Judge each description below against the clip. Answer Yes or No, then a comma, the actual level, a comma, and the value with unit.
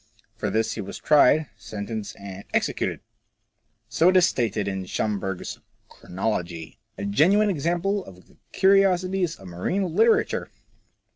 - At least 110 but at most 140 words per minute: Yes, slow, 135 wpm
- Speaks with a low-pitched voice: Yes, low, 120 Hz